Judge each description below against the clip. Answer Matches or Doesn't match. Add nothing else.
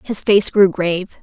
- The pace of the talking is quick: Doesn't match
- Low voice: Doesn't match